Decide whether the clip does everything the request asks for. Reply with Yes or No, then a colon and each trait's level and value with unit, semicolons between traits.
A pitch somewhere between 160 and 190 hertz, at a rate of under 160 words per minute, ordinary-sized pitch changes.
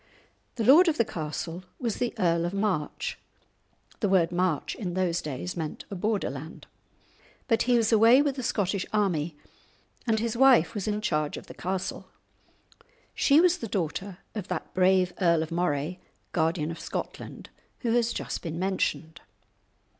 No: medium, 185 Hz; average, 165 wpm; average, 5.0 semitones